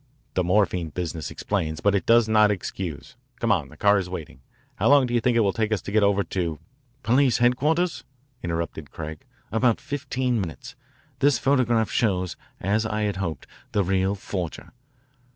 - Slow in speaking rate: No, average, 180 wpm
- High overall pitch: No, low, 105 Hz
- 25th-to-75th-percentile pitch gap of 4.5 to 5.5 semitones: Yes, average, 5.0 semitones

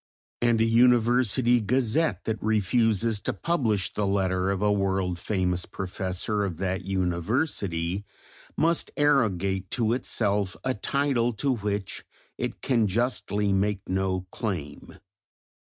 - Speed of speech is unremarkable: No, slow, 120 wpm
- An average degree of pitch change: Yes, average, 3.9 semitones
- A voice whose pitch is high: No, low, 105 Hz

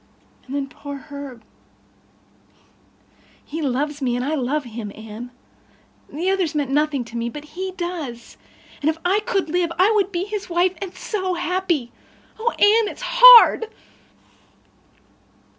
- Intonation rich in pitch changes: Yes, wide, 5.7 semitones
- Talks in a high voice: Yes, very high, 315 Hz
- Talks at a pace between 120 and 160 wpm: Yes, average, 140 wpm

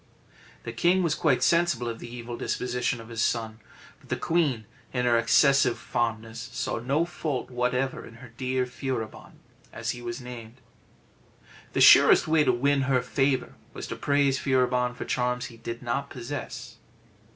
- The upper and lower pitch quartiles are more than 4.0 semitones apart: No, average, 2.7 semitones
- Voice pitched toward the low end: Yes, low, 125 Hz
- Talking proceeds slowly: No, average, 165 wpm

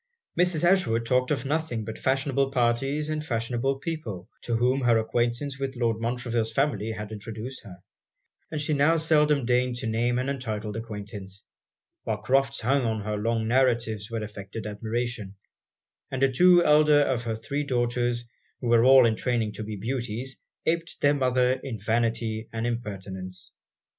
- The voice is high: No, low, 120 Hz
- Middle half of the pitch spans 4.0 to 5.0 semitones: No, average, 3.5 semitones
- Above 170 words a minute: No, average, 165 wpm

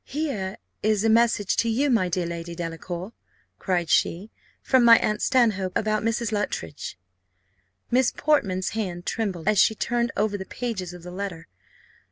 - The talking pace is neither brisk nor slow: Yes, average, 165 wpm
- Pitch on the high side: Yes, high, 205 Hz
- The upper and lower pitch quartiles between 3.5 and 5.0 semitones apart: Yes, average, 4.3 semitones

